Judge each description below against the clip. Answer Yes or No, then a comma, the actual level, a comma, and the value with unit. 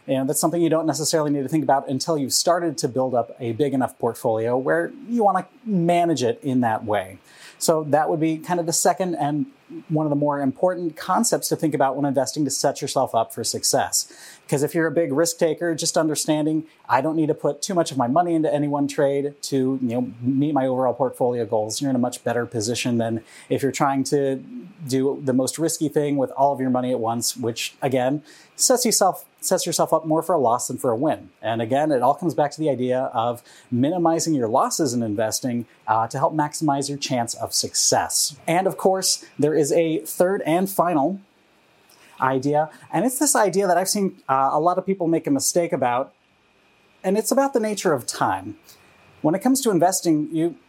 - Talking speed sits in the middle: No, fast, 220 wpm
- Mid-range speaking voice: Yes, medium, 150 Hz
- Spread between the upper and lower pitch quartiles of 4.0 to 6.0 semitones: Yes, average, 4.3 semitones